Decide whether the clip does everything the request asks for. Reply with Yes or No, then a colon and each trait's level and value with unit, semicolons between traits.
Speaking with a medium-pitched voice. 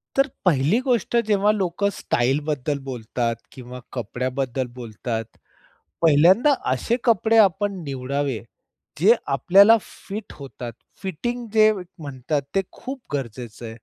Yes: medium, 150 Hz